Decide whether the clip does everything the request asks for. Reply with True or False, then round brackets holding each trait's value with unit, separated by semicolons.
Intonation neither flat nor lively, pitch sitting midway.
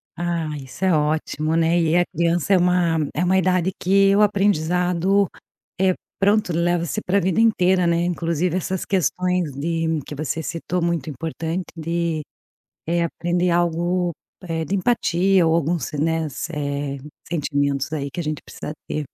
False (2.2 semitones; 170 Hz)